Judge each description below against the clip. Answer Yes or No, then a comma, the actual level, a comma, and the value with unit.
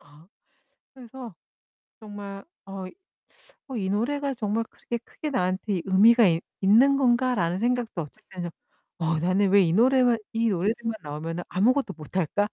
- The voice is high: Yes, high, 205 Hz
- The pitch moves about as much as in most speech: Yes, average, 4.8 semitones